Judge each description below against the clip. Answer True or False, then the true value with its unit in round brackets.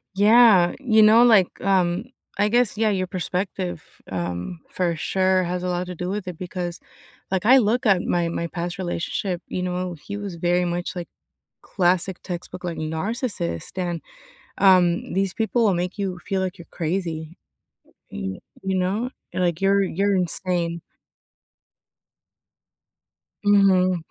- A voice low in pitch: False (185 Hz)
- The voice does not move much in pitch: True (2.2 semitones)